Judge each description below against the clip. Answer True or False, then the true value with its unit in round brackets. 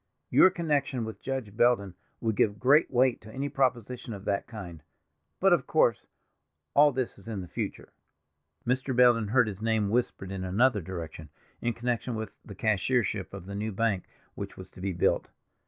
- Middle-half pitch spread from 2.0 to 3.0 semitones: False (4.1 semitones)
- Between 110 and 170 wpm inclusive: False (180 wpm)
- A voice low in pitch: True (110 Hz)